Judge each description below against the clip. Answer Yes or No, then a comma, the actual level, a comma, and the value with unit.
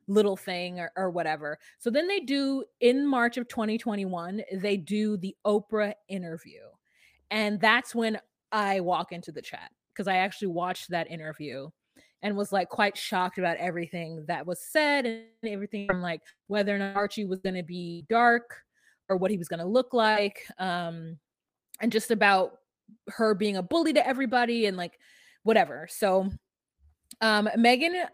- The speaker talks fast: No, average, 165 wpm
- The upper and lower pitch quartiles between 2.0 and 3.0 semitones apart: No, average, 4.1 semitones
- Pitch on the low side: No, high, 205 Hz